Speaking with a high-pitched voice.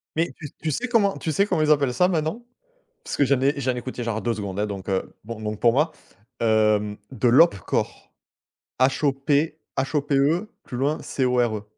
No: low, 135 Hz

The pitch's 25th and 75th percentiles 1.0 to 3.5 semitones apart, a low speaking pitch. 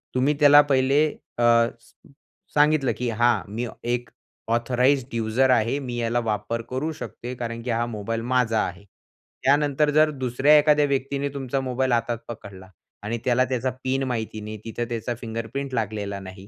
Yes: average, 2.9 semitones; low, 120 Hz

